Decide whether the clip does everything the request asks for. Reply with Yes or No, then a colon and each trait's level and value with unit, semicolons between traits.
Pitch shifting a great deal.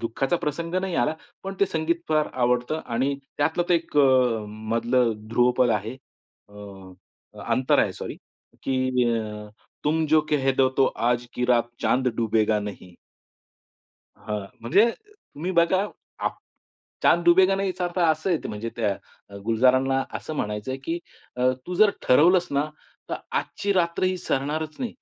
Yes: wide, 6.2 semitones